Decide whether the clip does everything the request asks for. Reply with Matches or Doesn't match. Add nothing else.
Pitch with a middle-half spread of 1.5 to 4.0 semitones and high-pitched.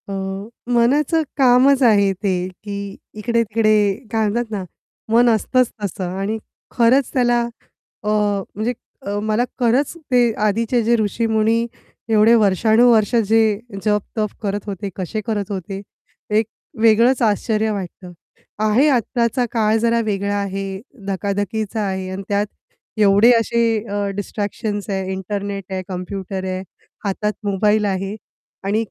Matches